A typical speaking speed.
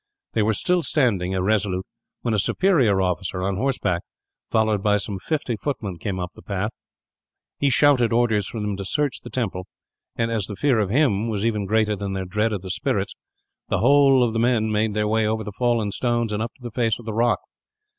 No: fast, 215 wpm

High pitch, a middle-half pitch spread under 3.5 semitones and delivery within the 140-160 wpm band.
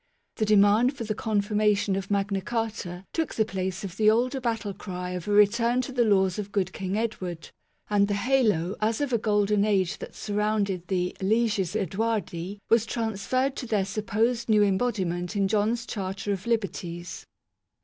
No: high, 205 Hz; average, 2.8 semitones; average, 180 wpm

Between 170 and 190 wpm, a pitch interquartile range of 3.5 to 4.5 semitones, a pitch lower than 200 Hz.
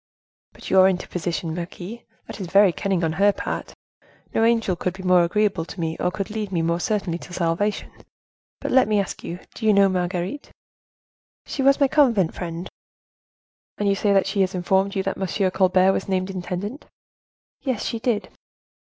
No: average, 185 wpm; average, 2.7 semitones; high, 190 Hz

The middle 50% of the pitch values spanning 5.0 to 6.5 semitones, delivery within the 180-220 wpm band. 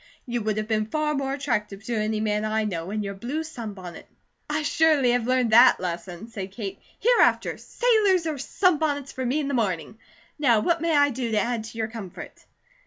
Yes: average, 5.3 semitones; average, 200 wpm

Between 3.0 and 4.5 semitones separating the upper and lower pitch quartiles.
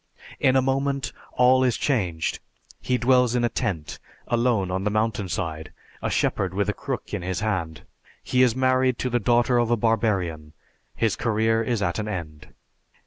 No: average, 4.9 semitones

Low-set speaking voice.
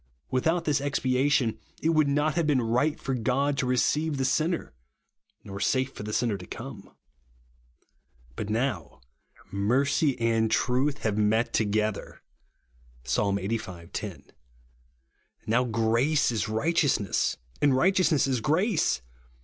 Yes: low, 125 Hz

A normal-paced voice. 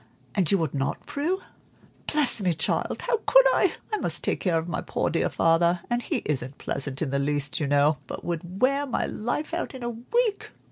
No: fast, 215 wpm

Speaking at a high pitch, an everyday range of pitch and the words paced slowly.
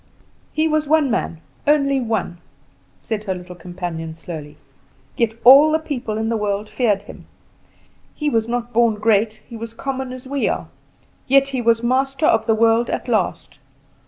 No: high, 230 Hz; average, 4.3 semitones; average, 170 wpm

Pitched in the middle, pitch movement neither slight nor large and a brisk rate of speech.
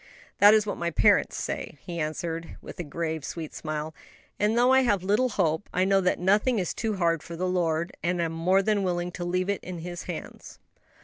Yes: medium, 180 Hz; average, 3.3 semitones; fast, 215 wpm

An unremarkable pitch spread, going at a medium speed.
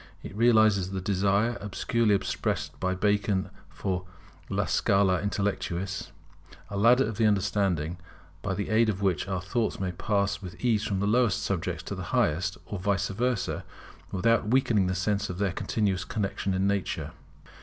No: narrow, 2.2 semitones; average, 165 wpm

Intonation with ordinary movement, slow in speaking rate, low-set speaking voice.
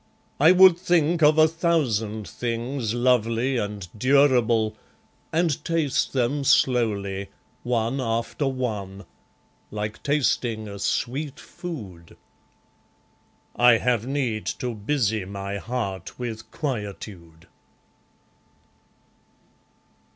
Yes: average, 4.9 semitones; slow, 90 wpm; low, 120 Hz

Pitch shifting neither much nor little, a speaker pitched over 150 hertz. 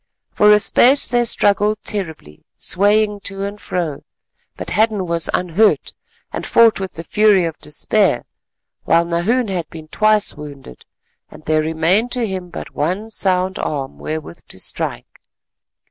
Yes: average, 4.6 semitones; high, 190 Hz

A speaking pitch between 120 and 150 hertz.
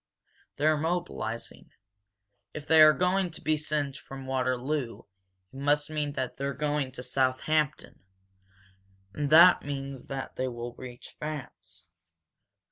Yes: medium, 140 Hz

